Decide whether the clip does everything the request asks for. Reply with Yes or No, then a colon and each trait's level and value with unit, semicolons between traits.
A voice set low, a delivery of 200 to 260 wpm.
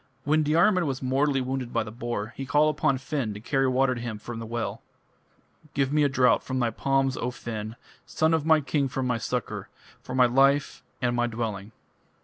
Yes: low, 130 Hz; fast, 205 wpm